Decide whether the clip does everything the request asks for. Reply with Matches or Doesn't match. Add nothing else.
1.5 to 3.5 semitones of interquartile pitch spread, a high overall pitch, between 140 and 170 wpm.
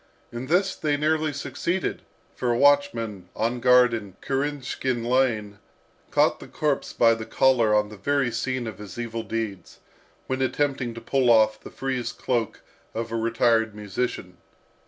Doesn't match